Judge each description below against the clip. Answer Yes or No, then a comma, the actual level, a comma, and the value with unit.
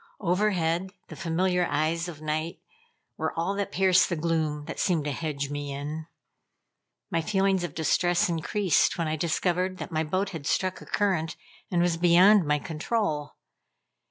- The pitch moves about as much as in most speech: Yes, average, 3.1 semitones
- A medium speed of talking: Yes, average, 160 wpm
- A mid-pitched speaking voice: Yes, medium, 170 Hz